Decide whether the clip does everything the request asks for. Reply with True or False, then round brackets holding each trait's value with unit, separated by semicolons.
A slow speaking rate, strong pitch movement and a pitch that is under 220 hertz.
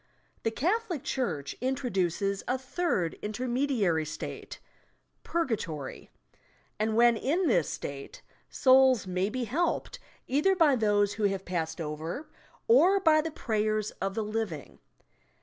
False (130 wpm; 6.5 semitones; 225 Hz)